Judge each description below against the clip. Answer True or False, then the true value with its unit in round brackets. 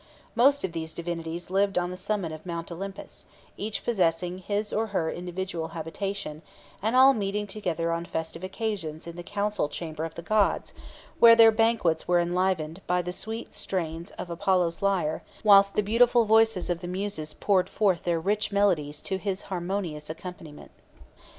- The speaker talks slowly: False (170 wpm)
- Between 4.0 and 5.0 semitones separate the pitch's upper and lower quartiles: False (3.5 semitones)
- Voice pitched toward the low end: False (185 Hz)